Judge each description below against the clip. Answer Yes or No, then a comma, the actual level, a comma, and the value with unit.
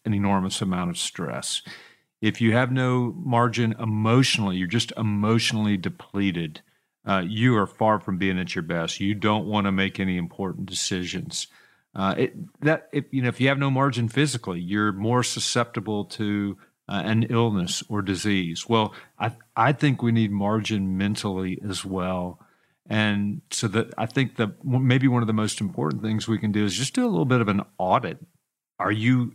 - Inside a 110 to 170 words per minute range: No, average, 185 wpm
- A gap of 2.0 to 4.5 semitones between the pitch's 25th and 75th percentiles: Yes, average, 3.4 semitones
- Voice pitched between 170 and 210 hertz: No, low, 110 Hz